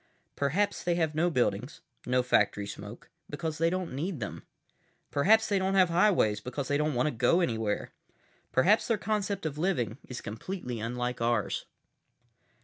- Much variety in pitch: Yes, wide, 7.0 semitones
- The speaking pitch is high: No, medium, 150 Hz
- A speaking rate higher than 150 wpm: Yes, average, 160 wpm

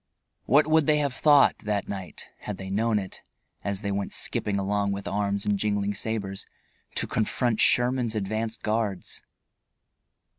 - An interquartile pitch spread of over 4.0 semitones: No, narrow, 2.5 semitones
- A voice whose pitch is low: Yes, low, 105 Hz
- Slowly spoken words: No, average, 150 wpm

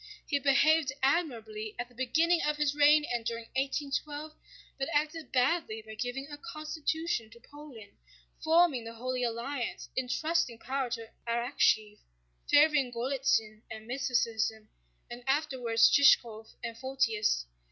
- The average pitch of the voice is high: Yes, very high, 260 Hz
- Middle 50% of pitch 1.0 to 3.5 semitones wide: No, average, 4.4 semitones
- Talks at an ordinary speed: No, slow, 130 wpm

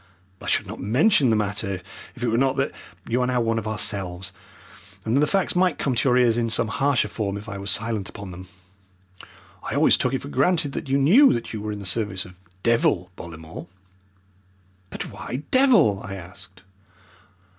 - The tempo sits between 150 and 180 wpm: No, average, 200 wpm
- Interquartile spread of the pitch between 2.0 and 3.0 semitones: No, average, 5.2 semitones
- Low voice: Yes, low, 115 Hz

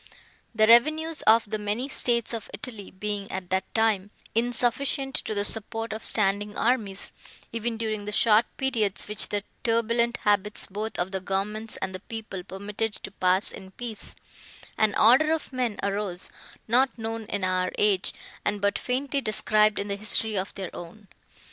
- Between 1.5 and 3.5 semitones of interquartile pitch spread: Yes, narrow, 2.6 semitones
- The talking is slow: No, average, 165 wpm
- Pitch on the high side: Yes, high, 215 Hz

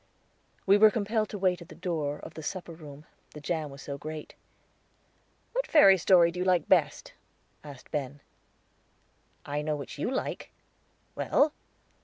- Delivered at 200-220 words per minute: No, average, 160 wpm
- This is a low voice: No, medium, 170 Hz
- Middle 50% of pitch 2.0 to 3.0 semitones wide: No, average, 4.6 semitones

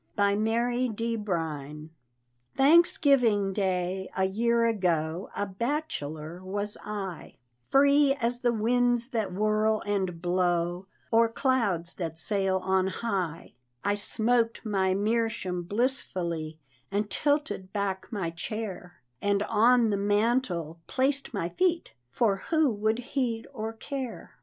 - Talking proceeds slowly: Yes, slow, 125 wpm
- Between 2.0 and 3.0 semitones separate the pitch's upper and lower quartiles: No, average, 4.2 semitones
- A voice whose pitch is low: No, high, 205 Hz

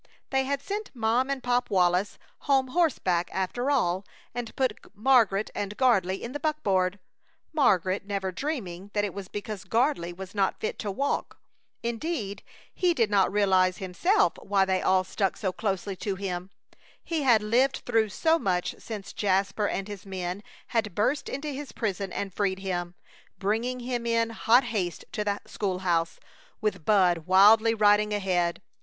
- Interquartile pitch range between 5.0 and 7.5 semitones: No, average, 4.5 semitones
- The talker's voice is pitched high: Yes, high, 205 Hz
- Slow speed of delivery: No, average, 165 wpm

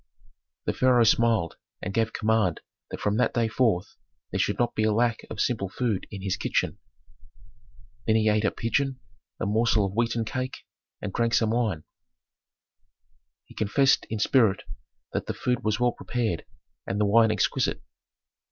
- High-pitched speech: No, low, 110 Hz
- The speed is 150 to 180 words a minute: Yes, average, 165 wpm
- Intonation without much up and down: Yes, narrow, 2.3 semitones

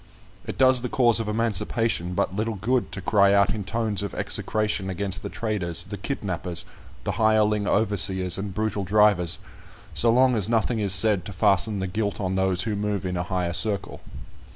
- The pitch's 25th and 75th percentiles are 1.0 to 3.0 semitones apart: Yes, narrow, 2.6 semitones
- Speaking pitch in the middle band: No, low, 100 Hz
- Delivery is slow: No, average, 185 wpm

